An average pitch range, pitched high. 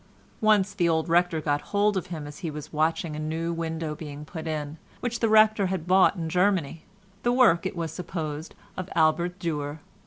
No: average, 3.4 semitones; medium, 165 Hz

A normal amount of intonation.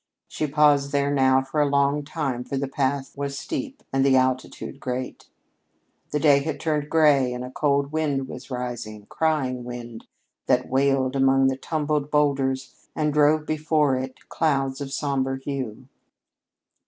No: narrow, 2.1 semitones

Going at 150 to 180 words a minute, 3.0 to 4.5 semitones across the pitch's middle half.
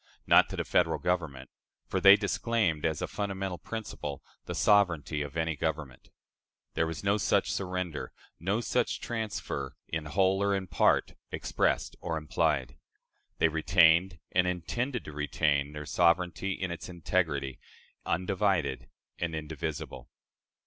No: slow, 135 wpm; average, 4.1 semitones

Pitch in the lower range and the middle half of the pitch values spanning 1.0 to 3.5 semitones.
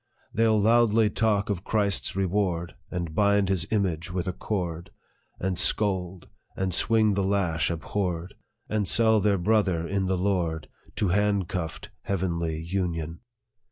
Yes: very low, 95 Hz; average, 3.1 semitones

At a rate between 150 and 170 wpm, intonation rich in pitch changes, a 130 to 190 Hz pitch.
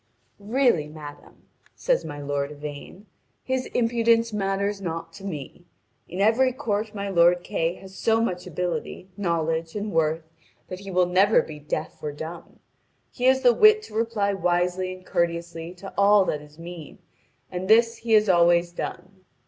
No: average, 165 wpm; average, 4.2 semitones; medium, 185 Hz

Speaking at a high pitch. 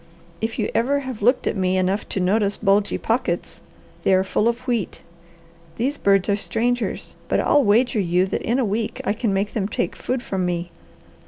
Yes: high, 210 Hz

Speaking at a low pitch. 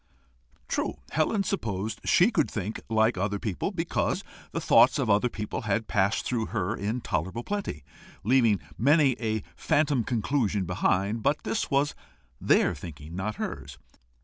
Yes: low, 110 Hz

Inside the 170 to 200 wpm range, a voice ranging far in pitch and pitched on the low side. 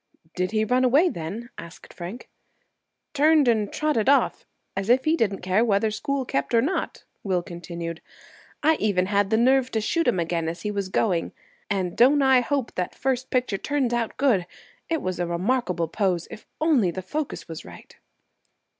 No: average, 180 wpm; wide, 6.3 semitones; high, 215 Hz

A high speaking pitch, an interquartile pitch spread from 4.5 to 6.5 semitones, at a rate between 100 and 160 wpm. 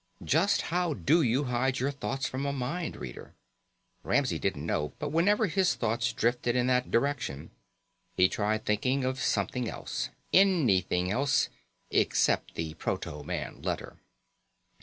No: low, 130 Hz; average, 4.8 semitones; average, 140 wpm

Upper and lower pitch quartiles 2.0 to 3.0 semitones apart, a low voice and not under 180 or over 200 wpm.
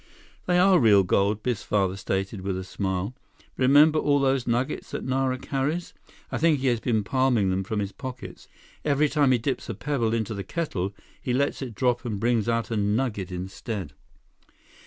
No: average, 5.1 semitones; low, 120 Hz; average, 185 wpm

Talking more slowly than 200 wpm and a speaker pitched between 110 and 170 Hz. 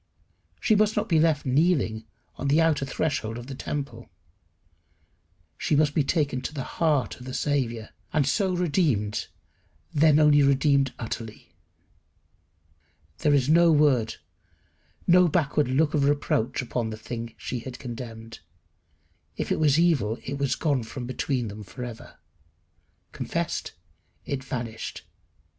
Yes: average, 140 wpm; medium, 140 Hz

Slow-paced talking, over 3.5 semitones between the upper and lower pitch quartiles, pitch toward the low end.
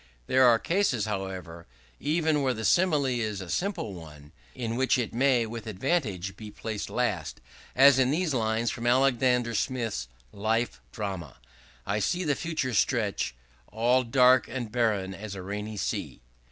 No: average, 155 wpm; average, 4.3 semitones; low, 115 Hz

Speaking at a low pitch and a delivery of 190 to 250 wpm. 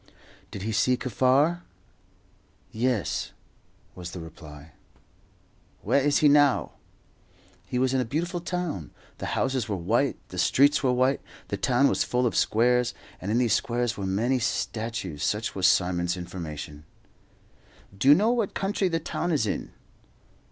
No: low, 120 Hz; average, 150 wpm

